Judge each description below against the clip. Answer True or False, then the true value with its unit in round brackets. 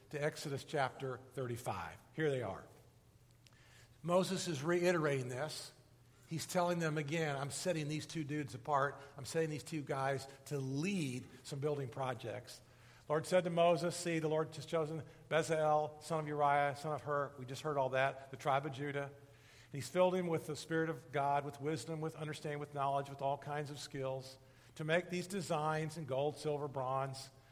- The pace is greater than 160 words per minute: True (180 wpm)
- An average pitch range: True (3.0 semitones)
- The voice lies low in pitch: False (145 Hz)